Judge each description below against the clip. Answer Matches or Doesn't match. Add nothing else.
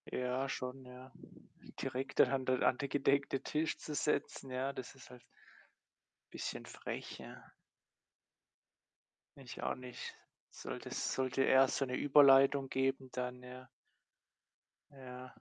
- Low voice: Matches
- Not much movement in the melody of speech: Matches